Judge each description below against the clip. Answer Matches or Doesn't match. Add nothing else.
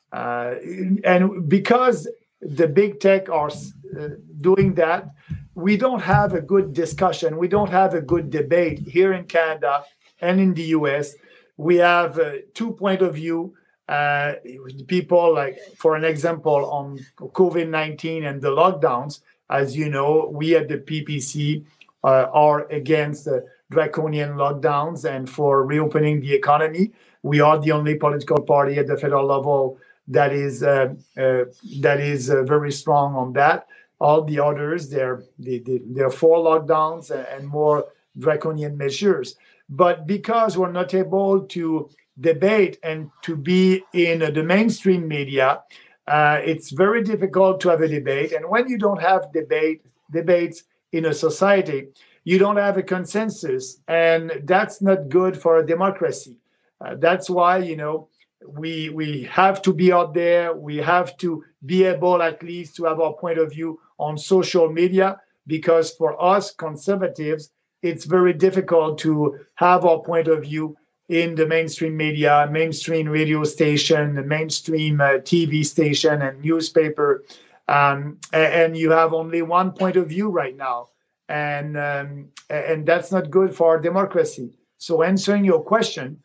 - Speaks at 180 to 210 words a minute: Doesn't match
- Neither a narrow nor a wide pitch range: Matches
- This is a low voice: Doesn't match